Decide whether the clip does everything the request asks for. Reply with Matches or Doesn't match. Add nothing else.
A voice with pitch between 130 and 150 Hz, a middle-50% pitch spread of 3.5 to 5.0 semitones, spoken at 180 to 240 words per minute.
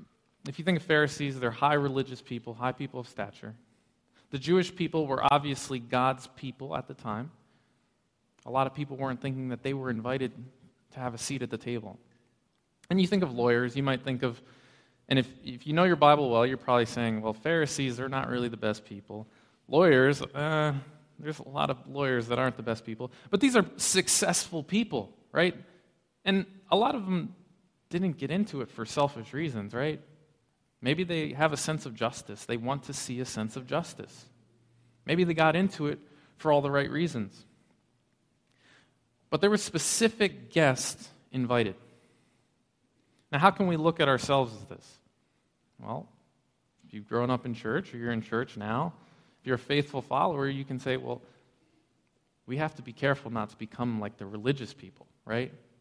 Matches